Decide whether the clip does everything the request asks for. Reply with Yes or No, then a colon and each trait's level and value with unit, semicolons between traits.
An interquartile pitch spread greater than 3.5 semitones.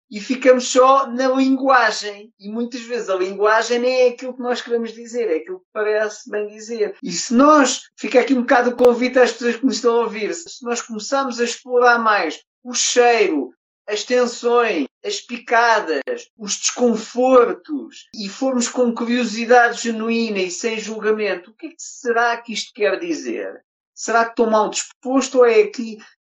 No: average, 2.7 semitones